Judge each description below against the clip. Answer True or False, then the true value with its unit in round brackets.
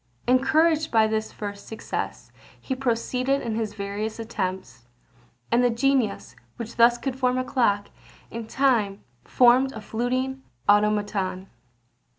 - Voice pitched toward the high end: True (230 Hz)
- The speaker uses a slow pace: True (130 wpm)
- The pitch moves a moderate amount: True (3.6 semitones)